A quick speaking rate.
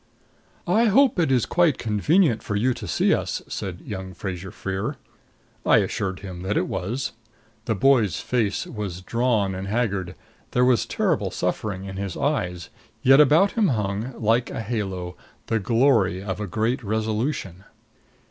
No: average, 155 wpm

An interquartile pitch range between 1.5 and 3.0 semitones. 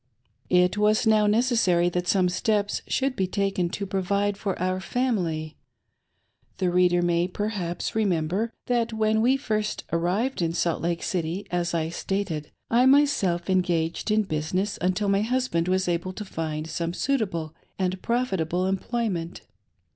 No: average, 3.8 semitones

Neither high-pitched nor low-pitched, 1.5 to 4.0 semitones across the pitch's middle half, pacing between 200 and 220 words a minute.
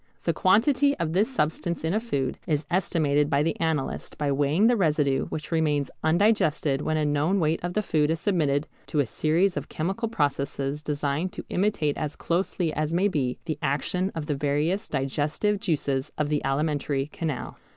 No: medium, 155 Hz; average, 3.7 semitones; average, 180 wpm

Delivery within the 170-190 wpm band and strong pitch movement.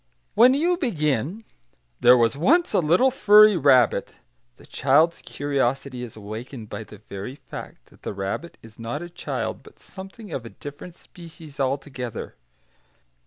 No: average, 150 wpm; wide, 7.0 semitones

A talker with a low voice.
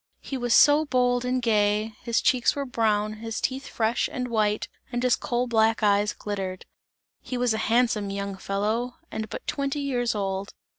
No: high, 230 Hz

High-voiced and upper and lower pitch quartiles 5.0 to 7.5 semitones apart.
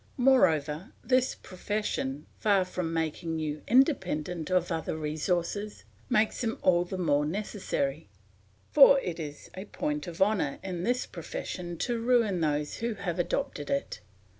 No: medium, 180 Hz; wide, 5.4 semitones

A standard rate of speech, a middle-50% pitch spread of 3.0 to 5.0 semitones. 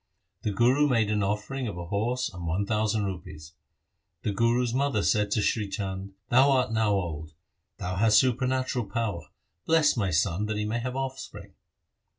Yes: average, 175 wpm; average, 4.2 semitones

